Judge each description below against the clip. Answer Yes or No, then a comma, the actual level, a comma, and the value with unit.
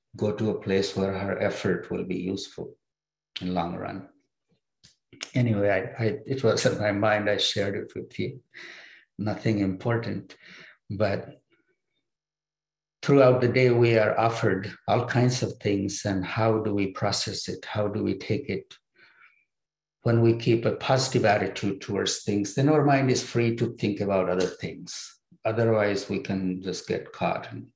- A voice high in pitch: No, low, 105 Hz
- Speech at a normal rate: Yes, average, 165 wpm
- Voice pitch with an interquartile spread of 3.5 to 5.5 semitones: No, average, 3.0 semitones